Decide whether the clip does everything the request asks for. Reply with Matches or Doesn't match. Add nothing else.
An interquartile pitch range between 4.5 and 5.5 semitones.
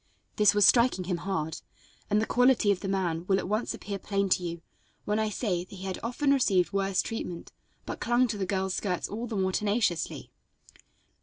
Doesn't match